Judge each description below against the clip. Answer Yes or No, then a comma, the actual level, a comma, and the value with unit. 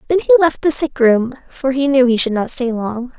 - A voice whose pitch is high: Yes, very high, 265 Hz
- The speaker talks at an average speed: No, fast, 265 wpm